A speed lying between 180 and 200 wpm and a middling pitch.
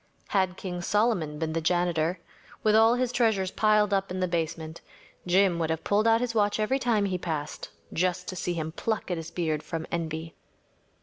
Yes: average, 195 wpm; medium, 180 Hz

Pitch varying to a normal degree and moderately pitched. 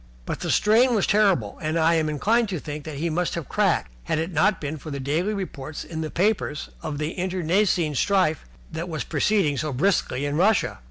Yes: average, 4.4 semitones; medium, 160 Hz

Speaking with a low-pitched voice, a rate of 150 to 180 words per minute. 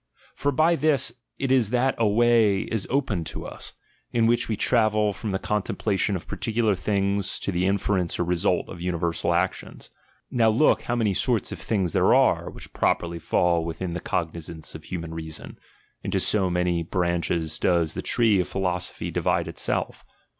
Yes: very low, 95 Hz; average, 175 wpm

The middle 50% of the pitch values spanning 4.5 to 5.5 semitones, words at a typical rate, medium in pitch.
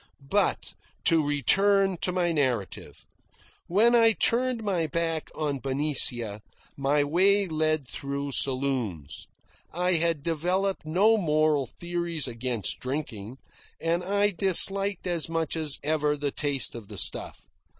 No: average, 4.8 semitones; slow, 130 wpm; medium, 155 Hz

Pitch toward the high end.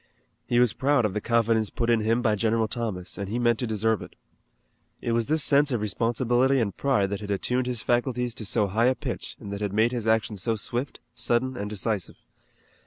No: low, 115 Hz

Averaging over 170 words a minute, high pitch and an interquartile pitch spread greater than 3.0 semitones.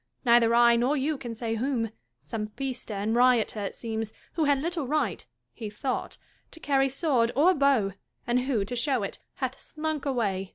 Yes: average, 190 wpm; high, 245 Hz; average, 3.9 semitones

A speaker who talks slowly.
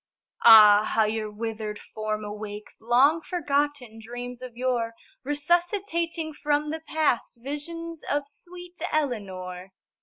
Yes: slow, 115 wpm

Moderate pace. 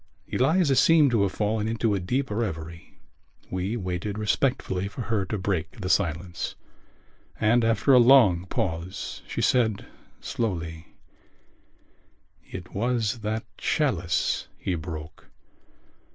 No: slow, 120 wpm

